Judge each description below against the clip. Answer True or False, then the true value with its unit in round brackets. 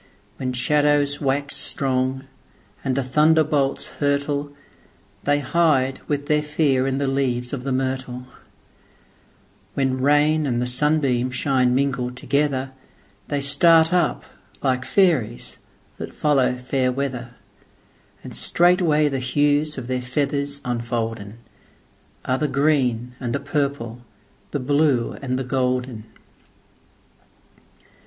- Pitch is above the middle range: False (135 Hz)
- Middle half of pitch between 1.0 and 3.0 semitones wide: True (2.4 semitones)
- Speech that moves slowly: True (110 wpm)